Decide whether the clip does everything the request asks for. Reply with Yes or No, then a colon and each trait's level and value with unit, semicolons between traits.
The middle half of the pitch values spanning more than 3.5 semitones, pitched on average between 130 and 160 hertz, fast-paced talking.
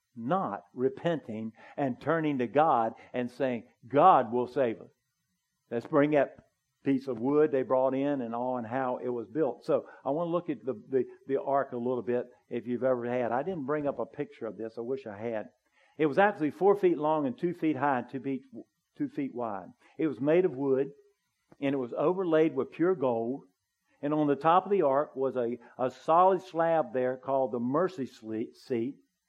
Yes: average, 4.2 semitones; low, 135 Hz; fast, 210 wpm